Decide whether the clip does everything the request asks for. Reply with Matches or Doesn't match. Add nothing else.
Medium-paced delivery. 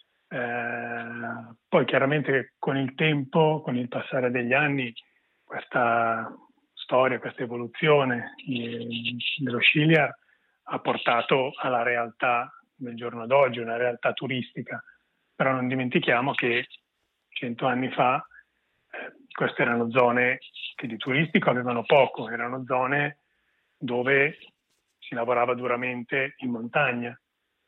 Doesn't match